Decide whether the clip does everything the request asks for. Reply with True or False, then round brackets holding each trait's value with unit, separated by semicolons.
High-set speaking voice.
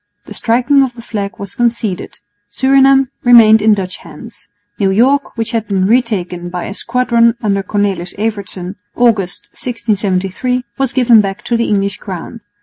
True (215 Hz)